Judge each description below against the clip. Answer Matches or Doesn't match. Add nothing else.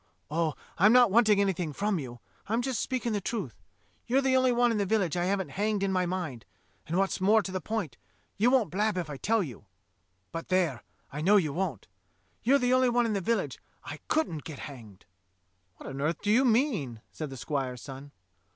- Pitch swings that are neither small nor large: Doesn't match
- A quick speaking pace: Matches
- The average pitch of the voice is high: Matches